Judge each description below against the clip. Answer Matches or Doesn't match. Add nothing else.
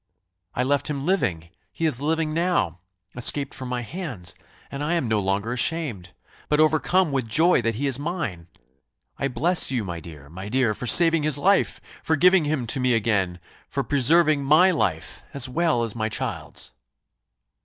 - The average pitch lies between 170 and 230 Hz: Doesn't match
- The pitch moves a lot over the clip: Matches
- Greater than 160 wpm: Matches